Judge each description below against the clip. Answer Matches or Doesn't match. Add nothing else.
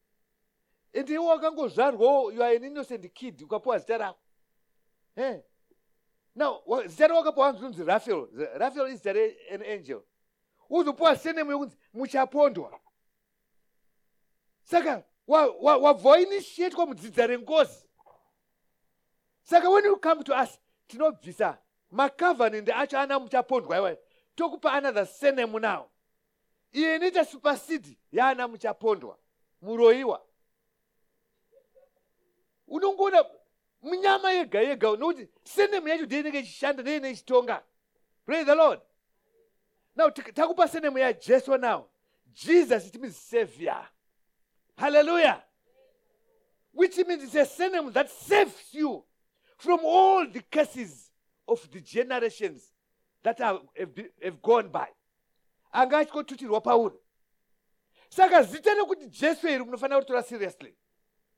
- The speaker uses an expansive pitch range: Matches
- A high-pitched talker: Matches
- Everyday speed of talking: Doesn't match